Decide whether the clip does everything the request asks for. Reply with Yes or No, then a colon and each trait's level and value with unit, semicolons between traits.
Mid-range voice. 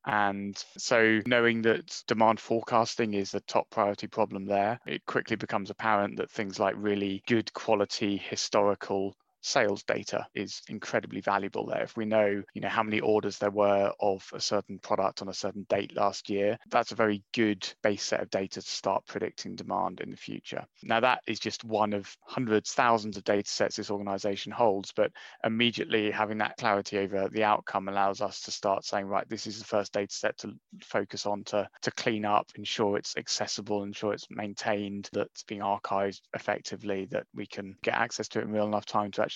No: low, 105 Hz